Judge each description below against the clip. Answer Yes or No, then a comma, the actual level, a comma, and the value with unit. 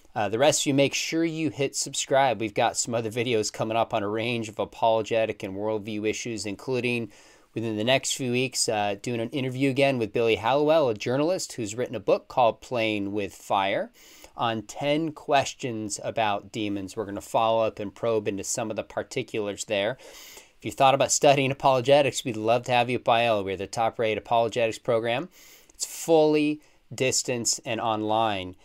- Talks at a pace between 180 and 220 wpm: Yes, average, 190 wpm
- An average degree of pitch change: Yes, average, 3.9 semitones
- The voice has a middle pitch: No, low, 115 Hz